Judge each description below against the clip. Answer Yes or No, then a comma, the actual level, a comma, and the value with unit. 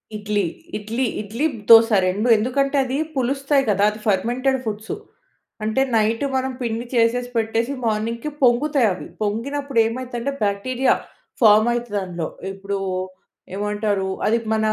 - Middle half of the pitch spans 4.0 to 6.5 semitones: No, average, 3.5 semitones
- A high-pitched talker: Yes, high, 230 Hz